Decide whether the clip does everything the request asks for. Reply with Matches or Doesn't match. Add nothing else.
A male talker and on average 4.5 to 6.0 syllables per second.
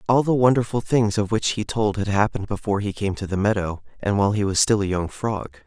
Doesn't match